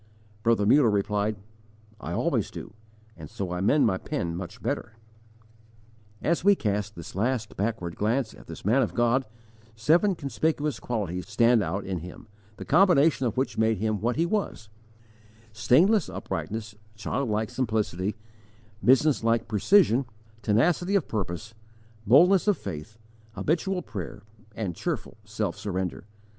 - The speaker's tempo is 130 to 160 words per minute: Yes, average, 140 wpm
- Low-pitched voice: Yes, low, 110 Hz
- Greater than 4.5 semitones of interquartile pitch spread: Yes, average, 5.2 semitones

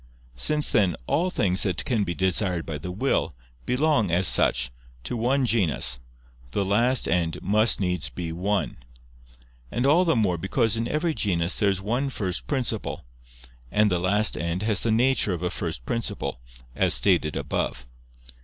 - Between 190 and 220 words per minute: No, average, 165 wpm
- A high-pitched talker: No, low, 100 Hz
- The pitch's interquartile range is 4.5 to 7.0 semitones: Yes, average, 5.0 semitones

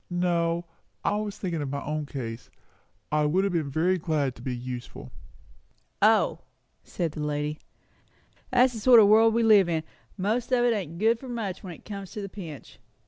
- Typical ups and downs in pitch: No, wide, 6.0 semitones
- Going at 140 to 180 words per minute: No, average, 195 wpm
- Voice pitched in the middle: Yes, medium, 175 Hz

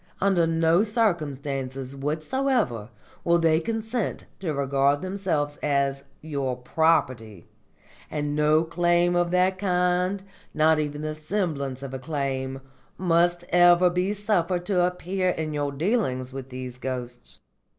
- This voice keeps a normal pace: No, slow, 130 wpm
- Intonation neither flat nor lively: Yes, average, 4.6 semitones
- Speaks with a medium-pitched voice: Yes, medium, 160 Hz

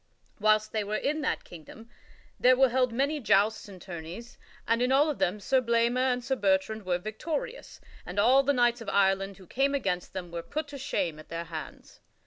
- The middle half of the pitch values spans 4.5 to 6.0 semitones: Yes, wide, 5.5 semitones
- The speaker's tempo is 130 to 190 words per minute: No, fast, 205 wpm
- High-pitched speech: Yes, high, 225 Hz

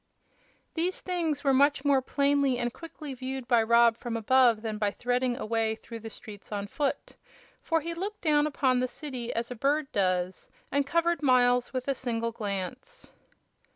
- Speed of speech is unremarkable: Yes, average, 180 wpm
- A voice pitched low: No, very high, 255 Hz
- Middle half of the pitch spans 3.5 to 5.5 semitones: Yes, average, 3.8 semitones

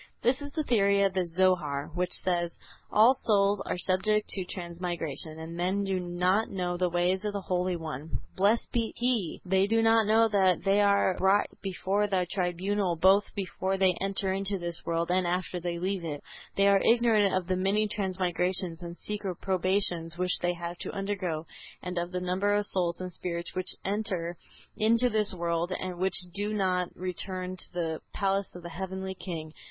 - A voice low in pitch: No, medium, 185 Hz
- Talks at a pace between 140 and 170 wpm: No, average, 185 wpm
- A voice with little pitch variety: Yes, narrow, 2.3 semitones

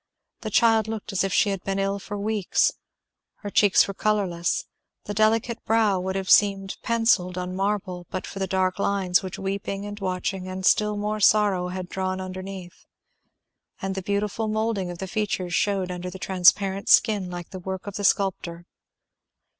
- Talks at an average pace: Yes, average, 180 wpm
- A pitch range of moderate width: No, narrow, 1.9 semitones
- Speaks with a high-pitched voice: Yes, high, 195 Hz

